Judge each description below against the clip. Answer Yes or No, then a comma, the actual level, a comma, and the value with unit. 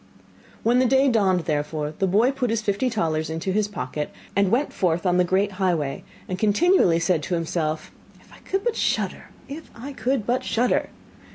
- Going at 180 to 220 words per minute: Yes, average, 190 wpm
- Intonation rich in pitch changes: Yes, wide, 6.6 semitones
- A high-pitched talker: Yes, high, 200 Hz